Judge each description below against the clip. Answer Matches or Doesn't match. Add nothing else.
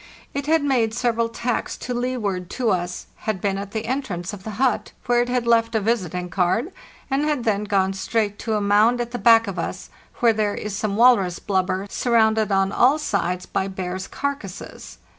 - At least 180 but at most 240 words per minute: Matches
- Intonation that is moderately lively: Matches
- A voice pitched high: Matches